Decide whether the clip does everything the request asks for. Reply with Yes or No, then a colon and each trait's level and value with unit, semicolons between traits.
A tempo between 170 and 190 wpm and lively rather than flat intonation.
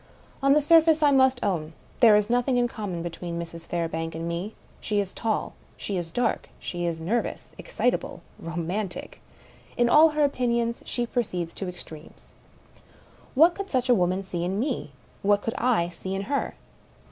Yes: average, 175 wpm; wide, 6.2 semitones